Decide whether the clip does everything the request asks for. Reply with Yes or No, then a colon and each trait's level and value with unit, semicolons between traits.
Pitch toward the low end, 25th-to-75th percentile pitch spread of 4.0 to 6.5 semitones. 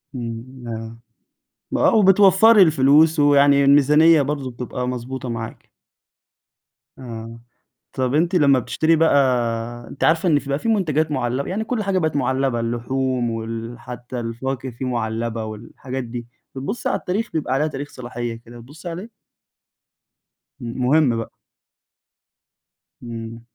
Yes: low, 130 Hz; average, 4.7 semitones